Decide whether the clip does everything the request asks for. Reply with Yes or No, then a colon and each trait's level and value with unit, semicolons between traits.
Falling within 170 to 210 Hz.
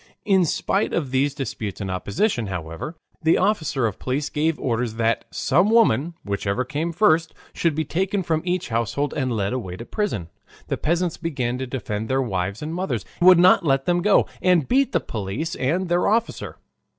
No: medium, 145 Hz